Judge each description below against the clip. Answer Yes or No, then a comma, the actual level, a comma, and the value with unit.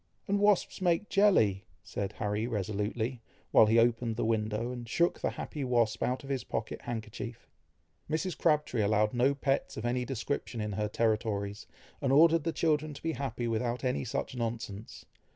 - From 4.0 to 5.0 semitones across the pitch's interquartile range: Yes, average, 4.4 semitones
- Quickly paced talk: No, average, 170 wpm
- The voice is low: Yes, low, 120 Hz